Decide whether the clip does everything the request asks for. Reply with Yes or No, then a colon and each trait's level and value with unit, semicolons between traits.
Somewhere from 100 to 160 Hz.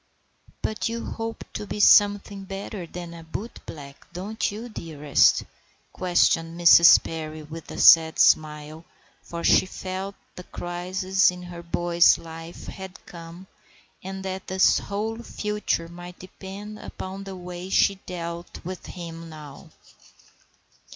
No: medium, 180 Hz